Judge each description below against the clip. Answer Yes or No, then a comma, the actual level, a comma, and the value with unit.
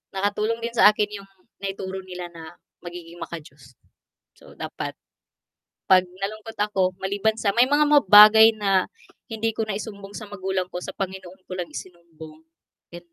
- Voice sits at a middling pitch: No, high, 195 Hz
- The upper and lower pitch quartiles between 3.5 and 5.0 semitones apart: No, average, 2.9 semitones